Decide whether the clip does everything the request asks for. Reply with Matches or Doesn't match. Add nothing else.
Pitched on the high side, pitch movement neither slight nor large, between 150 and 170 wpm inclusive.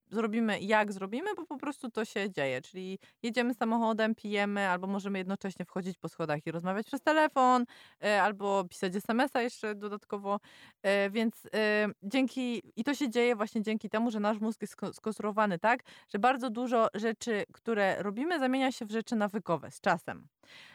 Matches